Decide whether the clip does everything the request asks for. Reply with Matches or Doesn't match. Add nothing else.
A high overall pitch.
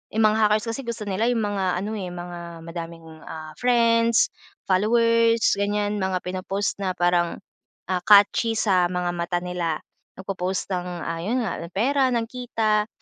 Matches